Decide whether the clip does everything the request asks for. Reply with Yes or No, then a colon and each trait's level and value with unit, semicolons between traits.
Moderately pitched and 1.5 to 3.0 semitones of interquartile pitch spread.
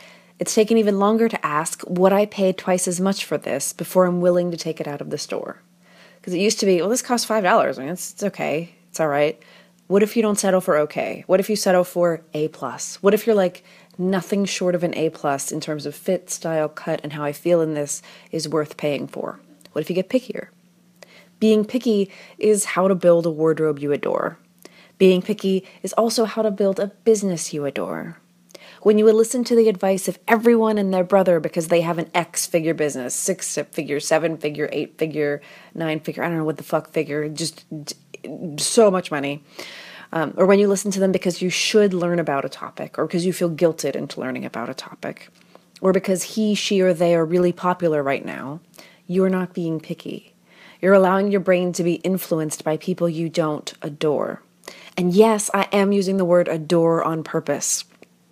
No: medium, 180 Hz; average, 3.5 semitones